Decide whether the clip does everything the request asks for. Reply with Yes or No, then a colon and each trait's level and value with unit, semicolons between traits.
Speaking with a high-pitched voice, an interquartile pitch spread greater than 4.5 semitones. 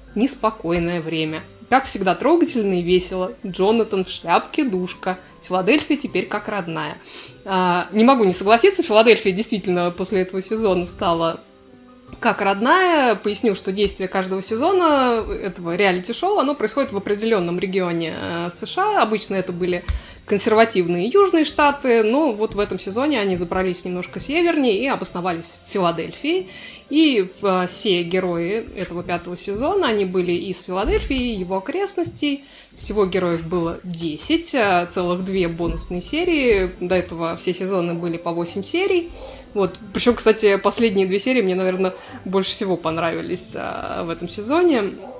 Yes: high, 195 Hz; average, 5.0 semitones